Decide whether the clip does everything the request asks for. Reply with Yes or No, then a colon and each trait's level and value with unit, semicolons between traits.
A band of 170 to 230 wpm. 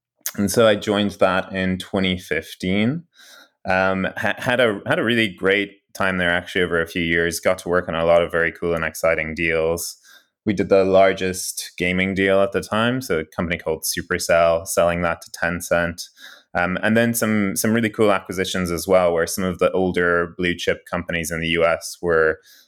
Yes: average, 195 wpm